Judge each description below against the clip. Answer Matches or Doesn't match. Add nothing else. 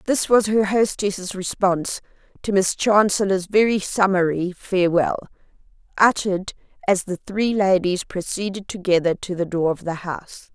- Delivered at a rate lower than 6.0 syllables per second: Matches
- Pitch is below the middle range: Doesn't match